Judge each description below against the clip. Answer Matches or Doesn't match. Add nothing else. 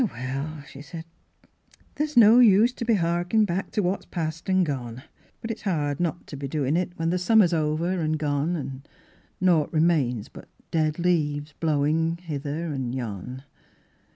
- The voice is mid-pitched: Matches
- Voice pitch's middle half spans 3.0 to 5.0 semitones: Matches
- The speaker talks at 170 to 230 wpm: Matches